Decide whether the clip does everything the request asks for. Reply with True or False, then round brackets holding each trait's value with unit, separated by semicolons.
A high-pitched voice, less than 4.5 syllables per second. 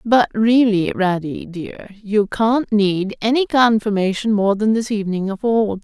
True (210 Hz; 4.2 syllables/s)